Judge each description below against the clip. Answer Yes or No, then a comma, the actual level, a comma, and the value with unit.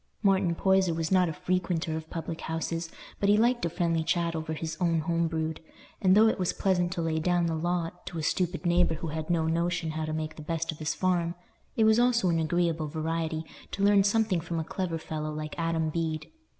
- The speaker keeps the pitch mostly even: Yes, narrow, 2.2 semitones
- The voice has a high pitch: No, medium, 165 Hz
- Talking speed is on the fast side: Yes, fast, 225 wpm